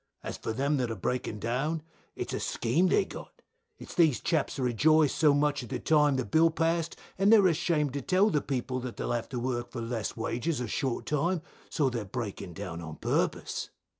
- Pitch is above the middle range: No, low, 135 Hz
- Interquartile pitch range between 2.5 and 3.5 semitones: No, average, 5.0 semitones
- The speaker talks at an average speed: No, fast, 220 wpm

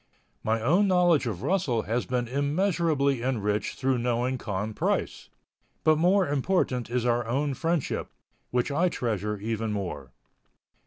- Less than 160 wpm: Yes, average, 140 wpm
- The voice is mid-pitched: No, low, 125 Hz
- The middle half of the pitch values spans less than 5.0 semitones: No, wide, 5.6 semitones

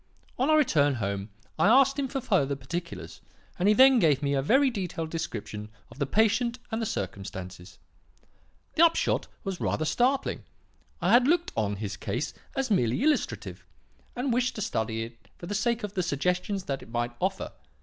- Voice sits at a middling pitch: Yes, medium, 180 Hz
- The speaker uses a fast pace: No, average, 180 wpm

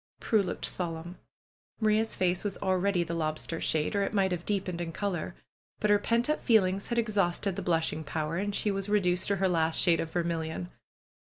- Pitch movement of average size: Yes, average, 3.3 semitones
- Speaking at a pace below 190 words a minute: No, fast, 205 wpm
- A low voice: No, medium, 185 Hz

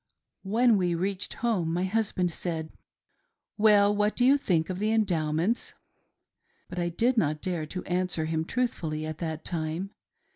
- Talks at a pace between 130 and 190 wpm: Yes, average, 160 wpm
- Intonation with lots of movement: No, average, 4.6 semitones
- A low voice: No, medium, 180 Hz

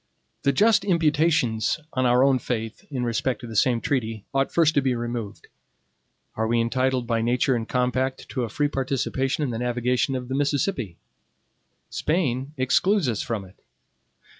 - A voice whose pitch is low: Yes, low, 130 Hz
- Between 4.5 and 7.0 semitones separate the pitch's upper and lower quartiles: No, average, 2.9 semitones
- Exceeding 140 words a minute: Yes, average, 165 wpm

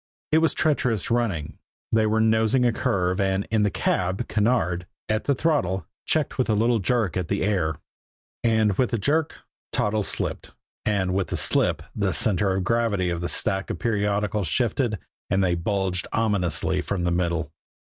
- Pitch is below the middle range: Yes, low, 105 Hz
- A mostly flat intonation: No, average, 3.8 semitones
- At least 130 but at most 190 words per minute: Yes, average, 175 wpm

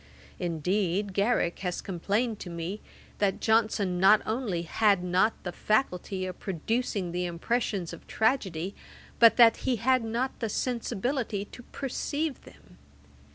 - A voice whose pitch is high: Yes, high, 205 Hz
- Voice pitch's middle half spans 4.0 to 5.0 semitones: Yes, average, 4.5 semitones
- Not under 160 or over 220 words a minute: No, slow, 135 wpm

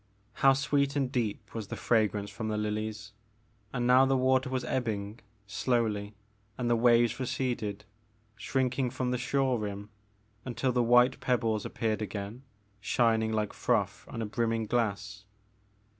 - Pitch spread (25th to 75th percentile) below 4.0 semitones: Yes, average, 2.9 semitones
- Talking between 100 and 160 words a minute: Yes, average, 145 wpm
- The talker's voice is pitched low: Yes, low, 115 Hz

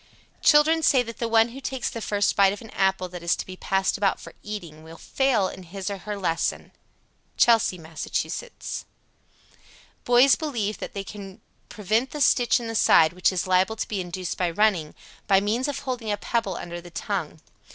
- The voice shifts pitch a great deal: No, average, 4.2 semitones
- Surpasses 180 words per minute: Yes, average, 200 wpm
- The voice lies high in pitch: Yes, high, 205 Hz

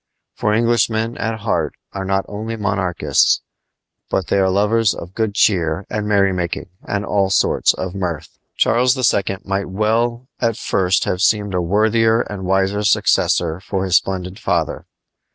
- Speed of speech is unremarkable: Yes, average, 150 wpm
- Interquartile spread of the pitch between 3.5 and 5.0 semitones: No, average, 3.0 semitones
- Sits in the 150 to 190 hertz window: No, low, 100 Hz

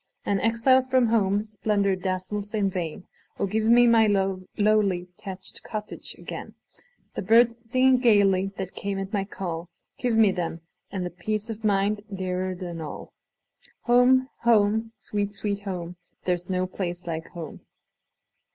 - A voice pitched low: No, high, 200 Hz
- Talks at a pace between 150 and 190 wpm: No, slow, 135 wpm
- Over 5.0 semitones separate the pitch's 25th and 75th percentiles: No, average, 3.3 semitones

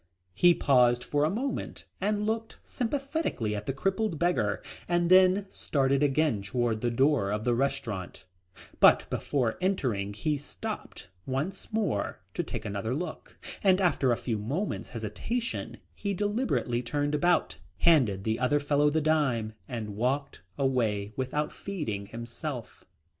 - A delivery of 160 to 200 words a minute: No, average, 140 wpm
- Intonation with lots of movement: Yes, wide, 7.6 semitones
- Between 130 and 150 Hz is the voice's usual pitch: Yes, medium, 140 Hz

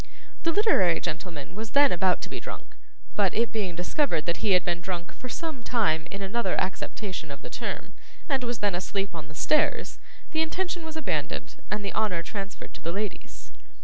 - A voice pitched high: Yes, high, 200 Hz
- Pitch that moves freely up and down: Yes, wide, 5.8 semitones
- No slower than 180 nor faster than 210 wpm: Yes, average, 195 wpm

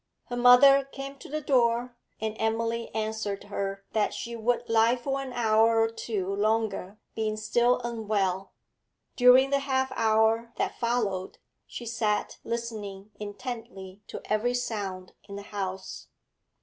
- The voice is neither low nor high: No, high, 225 Hz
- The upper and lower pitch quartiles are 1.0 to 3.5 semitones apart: Yes, average, 2.7 semitones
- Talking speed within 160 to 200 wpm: No, average, 140 wpm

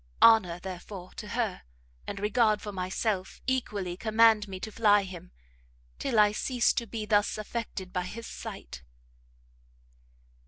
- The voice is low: No, high, 210 Hz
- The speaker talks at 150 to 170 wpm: No, average, 140 wpm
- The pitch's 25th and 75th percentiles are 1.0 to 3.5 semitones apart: Yes, average, 3.1 semitones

